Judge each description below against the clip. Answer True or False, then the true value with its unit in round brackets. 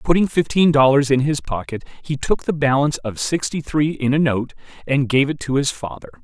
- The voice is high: False (140 Hz)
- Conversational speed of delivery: False (210 wpm)